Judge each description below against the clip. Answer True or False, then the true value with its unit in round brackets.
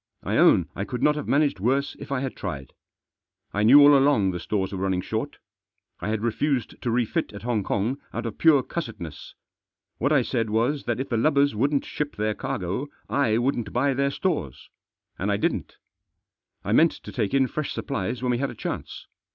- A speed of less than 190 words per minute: False (200 wpm)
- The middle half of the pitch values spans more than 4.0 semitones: True (4.8 semitones)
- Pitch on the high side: False (120 Hz)